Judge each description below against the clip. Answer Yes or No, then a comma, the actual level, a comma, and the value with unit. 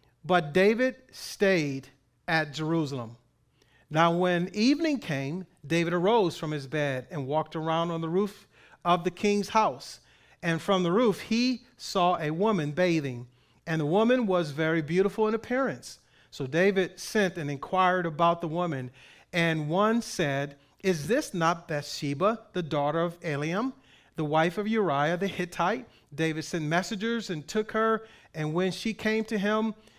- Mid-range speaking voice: Yes, medium, 175 Hz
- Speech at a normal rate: Yes, average, 155 wpm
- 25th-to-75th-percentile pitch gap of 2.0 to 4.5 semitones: No, average, 5.2 semitones